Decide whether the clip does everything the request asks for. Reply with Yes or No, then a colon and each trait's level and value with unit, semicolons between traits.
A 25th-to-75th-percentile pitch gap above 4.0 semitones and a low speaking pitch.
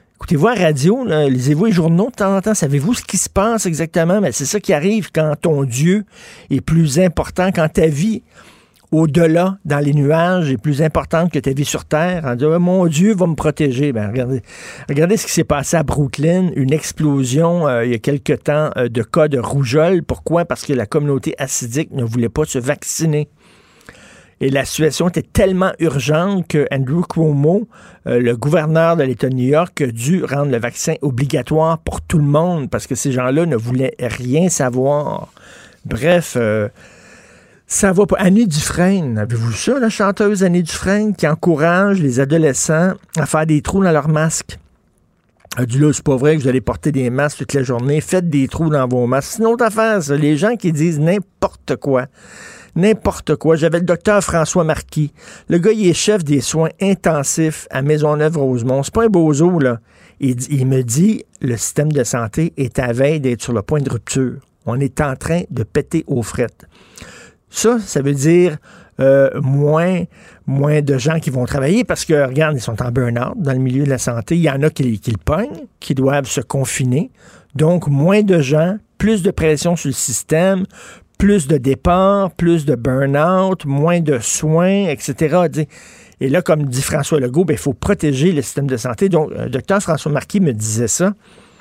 No: average, 4.5 semitones; medium, 155 Hz